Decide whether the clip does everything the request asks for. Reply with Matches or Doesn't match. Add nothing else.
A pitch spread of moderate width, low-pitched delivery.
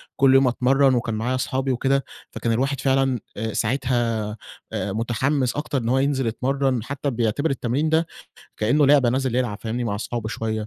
Matches